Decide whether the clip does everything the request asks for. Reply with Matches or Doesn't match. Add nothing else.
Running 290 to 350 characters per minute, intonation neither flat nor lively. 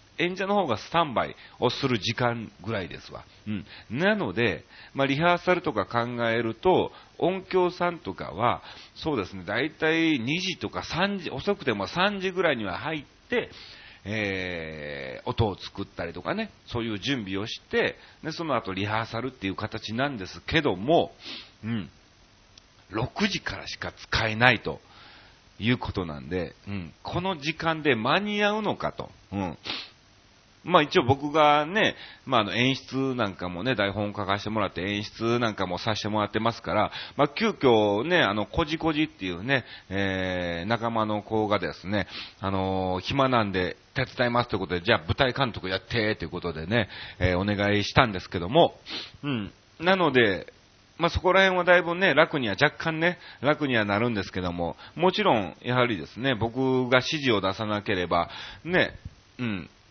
Doesn't match